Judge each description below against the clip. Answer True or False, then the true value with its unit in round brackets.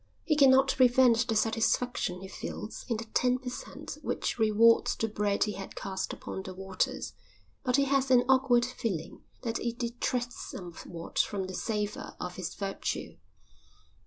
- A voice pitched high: True (230 Hz)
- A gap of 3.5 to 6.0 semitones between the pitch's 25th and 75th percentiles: True (4.2 semitones)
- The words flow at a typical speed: True (160 wpm)